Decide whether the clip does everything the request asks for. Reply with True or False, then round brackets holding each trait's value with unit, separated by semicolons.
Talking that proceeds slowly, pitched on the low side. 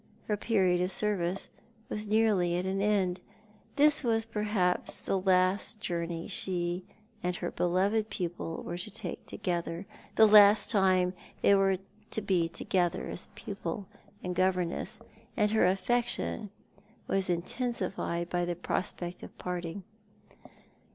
False (130 wpm; 185 Hz)